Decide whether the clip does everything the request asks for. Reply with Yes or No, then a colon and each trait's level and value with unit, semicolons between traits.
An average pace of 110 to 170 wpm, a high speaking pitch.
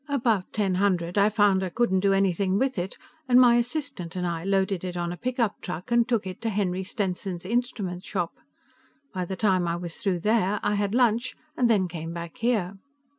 No: fast, 205 wpm; high, 195 Hz